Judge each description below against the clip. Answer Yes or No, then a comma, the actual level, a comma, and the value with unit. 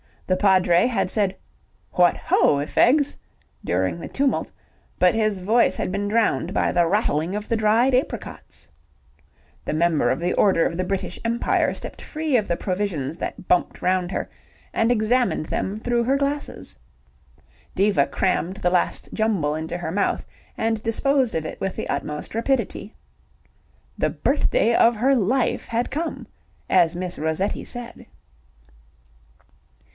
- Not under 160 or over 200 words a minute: No, average, 150 wpm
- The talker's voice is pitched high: Yes, high, 200 Hz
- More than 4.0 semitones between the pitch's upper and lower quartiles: Yes, average, 5.0 semitones